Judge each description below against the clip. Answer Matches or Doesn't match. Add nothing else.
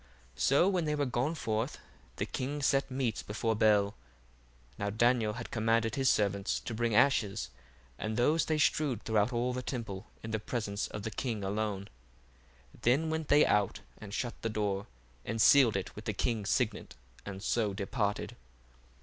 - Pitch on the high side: Doesn't match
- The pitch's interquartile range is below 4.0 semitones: Matches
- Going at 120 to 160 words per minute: Doesn't match